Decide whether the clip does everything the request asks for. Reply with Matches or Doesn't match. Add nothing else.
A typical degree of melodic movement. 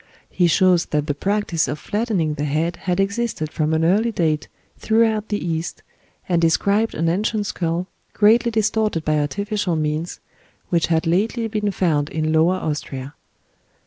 Matches